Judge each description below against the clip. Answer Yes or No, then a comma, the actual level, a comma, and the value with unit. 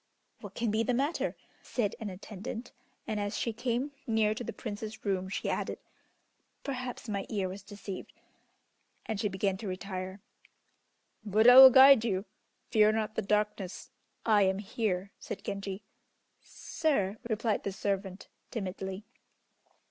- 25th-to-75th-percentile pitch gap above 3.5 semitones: No, average, 2.7 semitones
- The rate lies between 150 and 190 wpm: No, average, 140 wpm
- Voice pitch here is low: No, high, 210 Hz